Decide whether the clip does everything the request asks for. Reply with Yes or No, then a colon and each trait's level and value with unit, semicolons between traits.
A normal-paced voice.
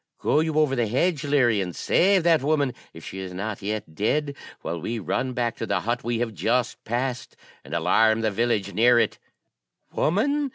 Yes: average, 195 wpm